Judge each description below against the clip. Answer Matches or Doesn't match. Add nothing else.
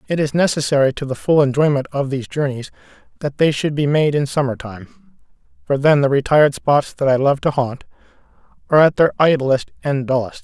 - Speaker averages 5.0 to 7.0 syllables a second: Matches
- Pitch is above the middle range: Doesn't match